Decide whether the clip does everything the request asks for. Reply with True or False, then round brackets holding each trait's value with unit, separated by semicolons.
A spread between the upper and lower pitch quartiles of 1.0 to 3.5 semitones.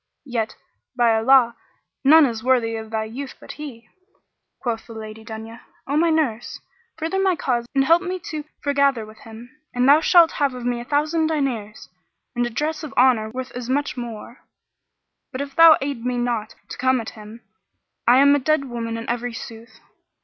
False (3.9 semitones)